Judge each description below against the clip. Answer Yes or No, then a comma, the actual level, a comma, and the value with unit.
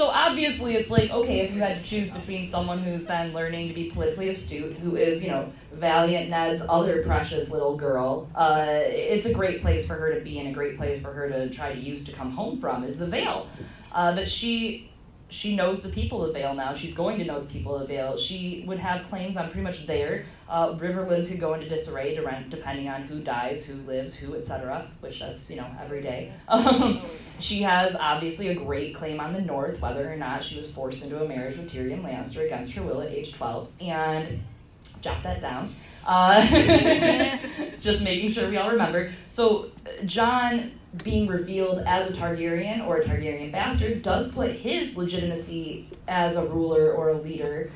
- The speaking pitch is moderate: Yes, medium, 170 Hz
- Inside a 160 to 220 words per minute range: Yes, fast, 205 wpm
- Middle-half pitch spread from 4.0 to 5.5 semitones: Yes, average, 4.4 semitones